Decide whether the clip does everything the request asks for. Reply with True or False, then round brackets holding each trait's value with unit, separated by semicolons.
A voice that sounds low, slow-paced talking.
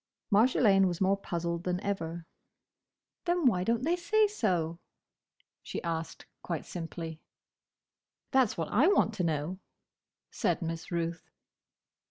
False (180 Hz; 125 wpm)